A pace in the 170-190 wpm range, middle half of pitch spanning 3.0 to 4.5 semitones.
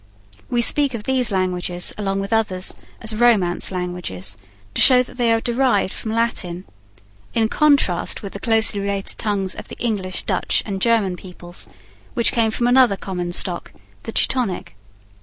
No: average, 160 wpm; average, 4.1 semitones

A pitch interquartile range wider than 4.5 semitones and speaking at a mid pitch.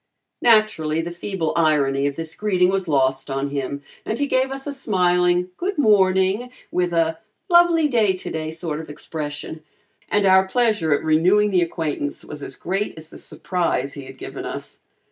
Yes: average, 5.2 semitones; medium, 175 Hz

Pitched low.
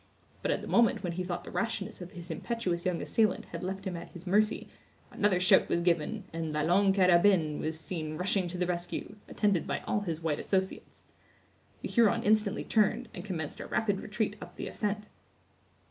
No: medium, 185 Hz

